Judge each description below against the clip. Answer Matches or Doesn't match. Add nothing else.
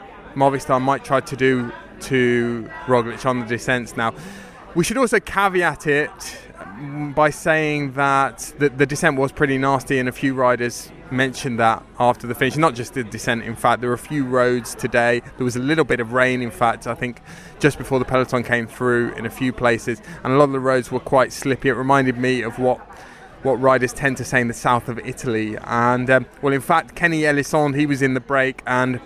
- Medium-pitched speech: Doesn't match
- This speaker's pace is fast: Matches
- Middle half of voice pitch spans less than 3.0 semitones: Matches